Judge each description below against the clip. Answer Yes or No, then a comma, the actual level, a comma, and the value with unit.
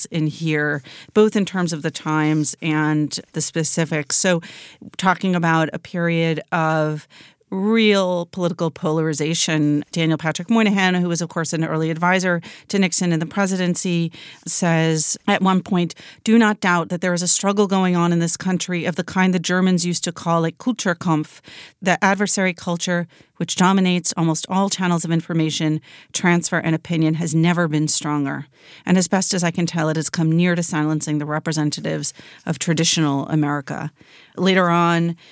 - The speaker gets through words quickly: No, average, 170 wpm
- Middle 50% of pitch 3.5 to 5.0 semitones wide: No, narrow, 2.5 semitones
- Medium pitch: Yes, medium, 170 Hz